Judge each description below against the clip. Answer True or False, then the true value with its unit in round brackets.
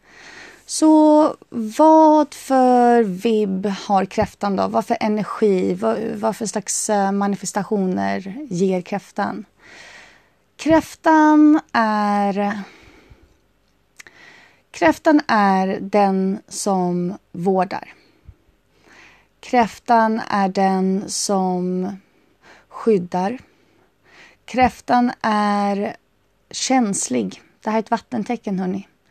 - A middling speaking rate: False (80 wpm)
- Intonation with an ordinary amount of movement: True (4.0 semitones)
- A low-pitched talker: False (210 Hz)